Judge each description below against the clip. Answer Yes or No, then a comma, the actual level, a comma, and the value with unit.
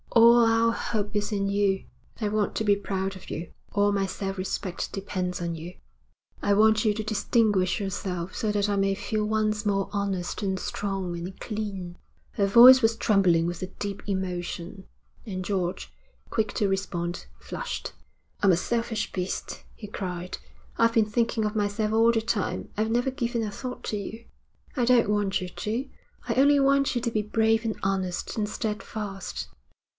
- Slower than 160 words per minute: No, average, 180 wpm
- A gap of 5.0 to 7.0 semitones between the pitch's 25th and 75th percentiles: No, average, 2.7 semitones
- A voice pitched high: Yes, high, 205 Hz